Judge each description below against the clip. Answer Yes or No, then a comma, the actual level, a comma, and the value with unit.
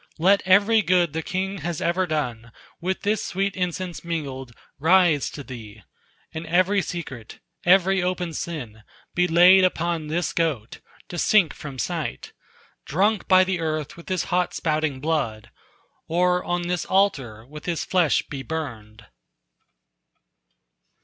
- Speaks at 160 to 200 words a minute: No, average, 140 wpm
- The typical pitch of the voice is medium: Yes, medium, 170 Hz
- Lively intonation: No, average, 3.9 semitones